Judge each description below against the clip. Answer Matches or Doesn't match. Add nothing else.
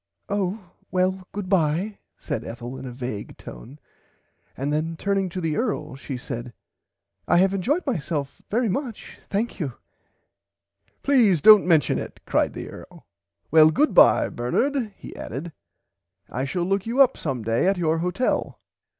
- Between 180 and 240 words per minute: Doesn't match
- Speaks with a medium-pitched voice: Matches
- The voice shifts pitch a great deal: Matches